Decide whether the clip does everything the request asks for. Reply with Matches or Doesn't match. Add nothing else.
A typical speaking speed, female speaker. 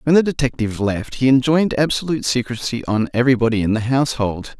Doesn't match